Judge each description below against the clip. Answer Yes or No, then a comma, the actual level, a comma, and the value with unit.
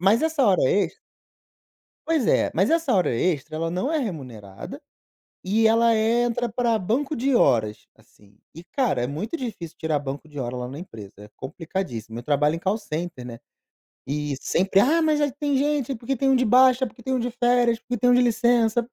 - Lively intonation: Yes, wide, 8.7 semitones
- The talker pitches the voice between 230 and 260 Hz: No, high, 215 Hz